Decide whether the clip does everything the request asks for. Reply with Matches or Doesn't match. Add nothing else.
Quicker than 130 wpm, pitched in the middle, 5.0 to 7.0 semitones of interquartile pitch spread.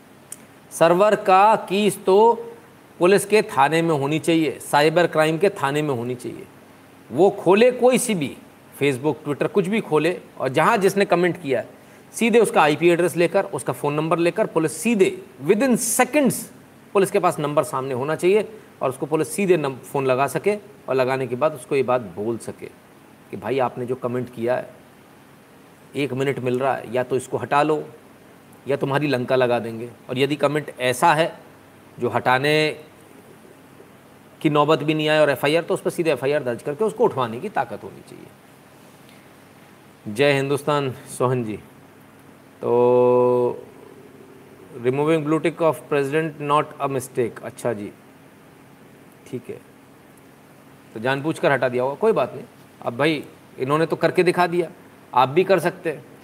Matches